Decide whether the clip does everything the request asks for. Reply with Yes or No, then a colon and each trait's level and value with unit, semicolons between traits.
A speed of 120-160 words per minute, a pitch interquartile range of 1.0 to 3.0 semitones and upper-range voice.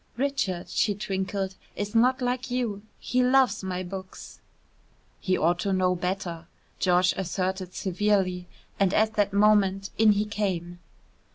Yes: average, 140 wpm; narrow, 2.5 semitones; high, 195 Hz